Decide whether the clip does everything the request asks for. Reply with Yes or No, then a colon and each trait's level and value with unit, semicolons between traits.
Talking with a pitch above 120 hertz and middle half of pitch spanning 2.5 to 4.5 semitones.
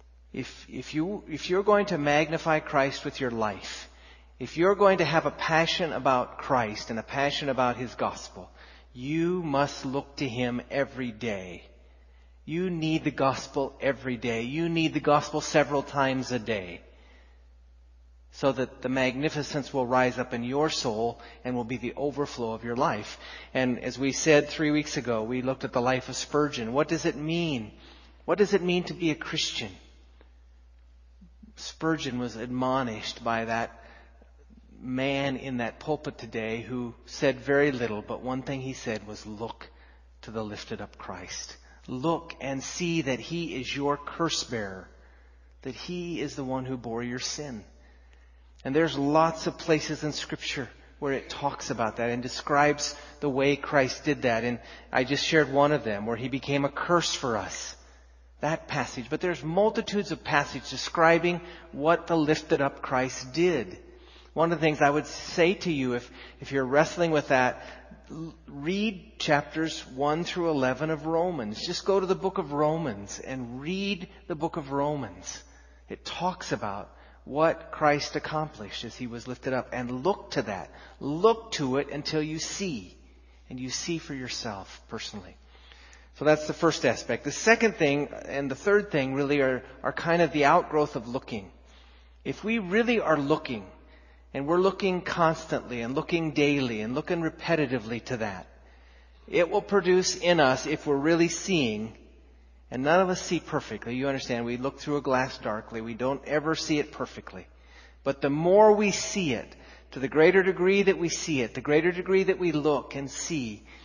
No: medium, 140 Hz; wide, 5.5 semitones